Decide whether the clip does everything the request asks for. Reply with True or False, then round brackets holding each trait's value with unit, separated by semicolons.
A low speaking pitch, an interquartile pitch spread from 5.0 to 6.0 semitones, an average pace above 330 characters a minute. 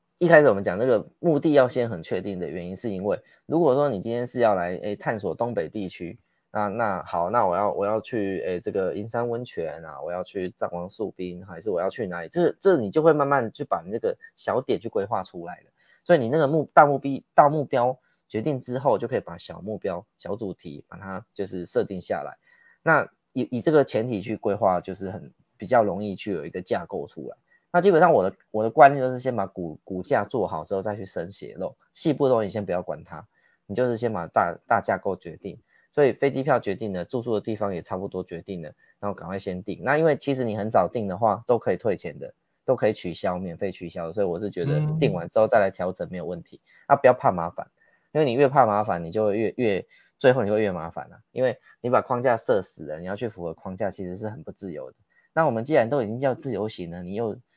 True (105 Hz; 5.5 semitones; 345 characters per minute)